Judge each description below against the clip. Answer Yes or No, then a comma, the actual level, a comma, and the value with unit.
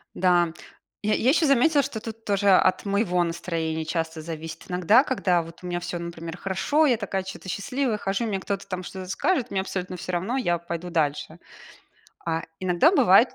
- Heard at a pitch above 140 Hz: Yes, medium, 185 Hz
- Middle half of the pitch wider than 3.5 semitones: Yes, average, 4.1 semitones